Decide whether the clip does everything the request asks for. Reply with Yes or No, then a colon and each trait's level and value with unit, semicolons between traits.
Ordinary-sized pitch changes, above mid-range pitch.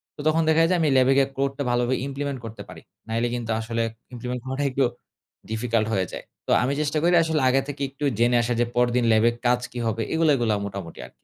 No: average, 3.2 semitones; low, 125 Hz